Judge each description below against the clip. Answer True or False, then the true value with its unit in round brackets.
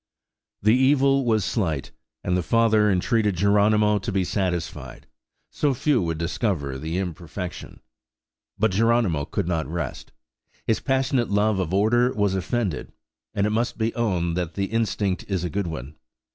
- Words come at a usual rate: True (155 wpm)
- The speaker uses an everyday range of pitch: True (4.7 semitones)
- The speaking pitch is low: True (100 Hz)